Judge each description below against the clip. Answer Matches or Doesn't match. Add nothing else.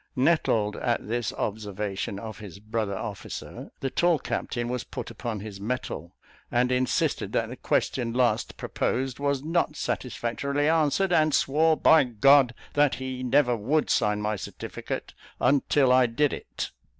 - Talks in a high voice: Doesn't match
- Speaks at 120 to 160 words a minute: Matches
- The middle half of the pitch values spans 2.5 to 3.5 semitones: Doesn't match